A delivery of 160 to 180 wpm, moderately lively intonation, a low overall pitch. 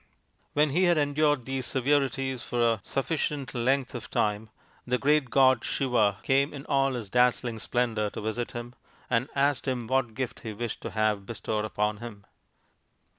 Yes: average, 170 wpm; average, 3.5 semitones; low, 125 Hz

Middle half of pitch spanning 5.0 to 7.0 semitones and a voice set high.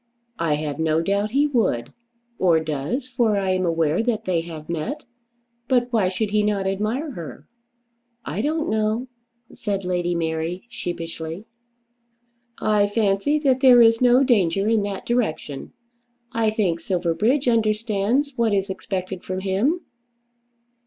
Yes: average, 5.3 semitones; high, 205 Hz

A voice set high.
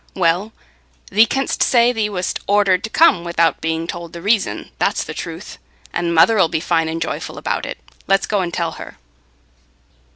No: medium, 180 Hz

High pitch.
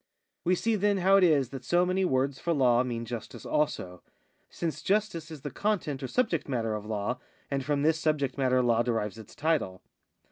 No: medium, 140 Hz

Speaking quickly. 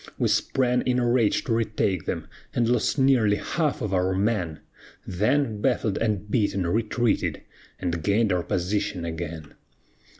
No: average, 145 wpm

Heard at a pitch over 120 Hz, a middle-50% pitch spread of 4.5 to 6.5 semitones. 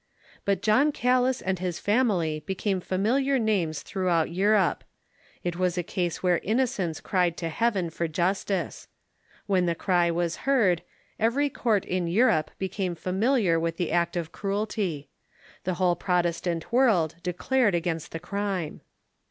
No: medium, 185 Hz; average, 3.8 semitones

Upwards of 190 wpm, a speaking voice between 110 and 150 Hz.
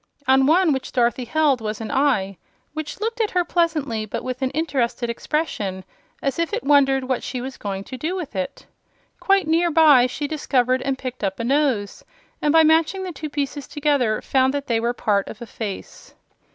No: average, 200 wpm; very high, 270 Hz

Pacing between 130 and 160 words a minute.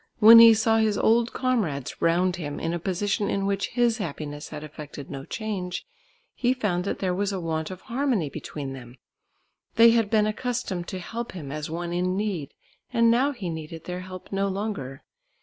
No: average, 190 wpm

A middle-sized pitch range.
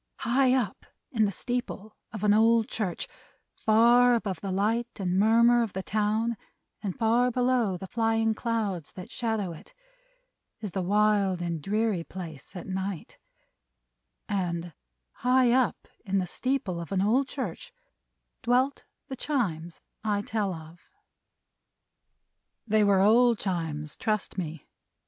Yes: average, 3.9 semitones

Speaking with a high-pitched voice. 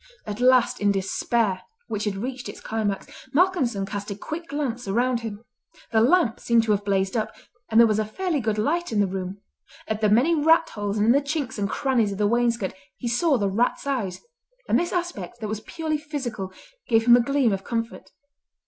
Yes: high, 230 Hz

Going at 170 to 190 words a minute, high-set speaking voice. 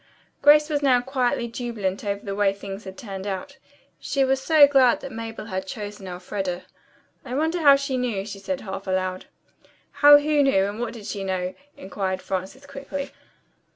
Yes: average, 175 wpm; high, 225 Hz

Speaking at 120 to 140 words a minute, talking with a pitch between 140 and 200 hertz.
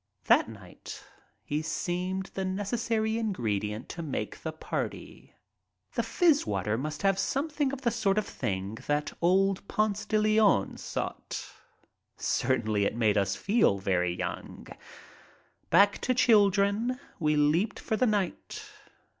Yes: slow, 135 wpm; high, 190 Hz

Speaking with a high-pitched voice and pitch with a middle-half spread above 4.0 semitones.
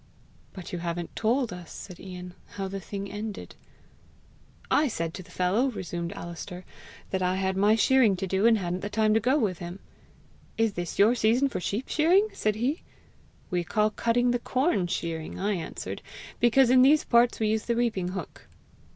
Yes: high, 205 Hz; average, 4.7 semitones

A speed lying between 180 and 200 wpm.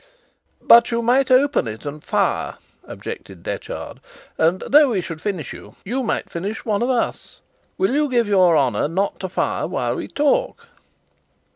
No: average, 165 wpm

